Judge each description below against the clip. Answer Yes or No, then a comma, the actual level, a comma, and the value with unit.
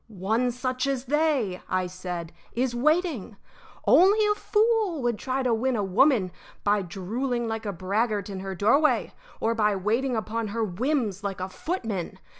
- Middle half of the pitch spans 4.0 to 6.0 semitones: Yes, average, 5.1 semitones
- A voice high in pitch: Yes, high, 230 Hz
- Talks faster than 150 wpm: Yes, average, 165 wpm